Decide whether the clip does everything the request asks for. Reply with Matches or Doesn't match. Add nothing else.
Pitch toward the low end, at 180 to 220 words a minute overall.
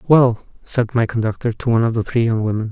Doesn't match